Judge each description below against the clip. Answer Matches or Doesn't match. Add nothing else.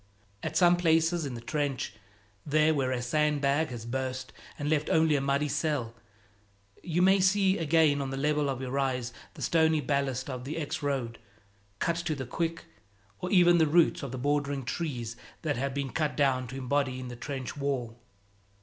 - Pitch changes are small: Doesn't match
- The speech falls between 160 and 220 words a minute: Matches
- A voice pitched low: Doesn't match